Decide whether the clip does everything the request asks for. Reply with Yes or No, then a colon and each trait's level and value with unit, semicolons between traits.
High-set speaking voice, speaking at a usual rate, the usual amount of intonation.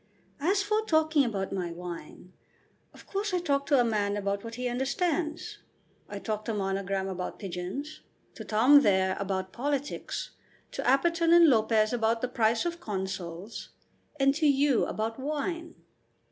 No: high, 240 Hz; average, 160 wpm; wide, 7.4 semitones